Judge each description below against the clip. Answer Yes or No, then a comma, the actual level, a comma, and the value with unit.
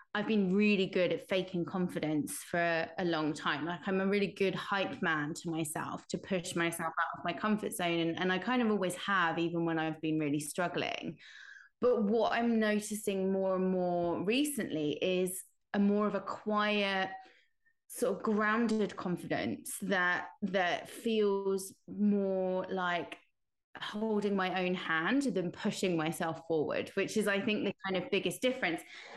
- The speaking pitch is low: No, high, 190 Hz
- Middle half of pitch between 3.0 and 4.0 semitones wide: Yes, average, 3.5 semitones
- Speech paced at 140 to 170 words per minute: Yes, average, 165 wpm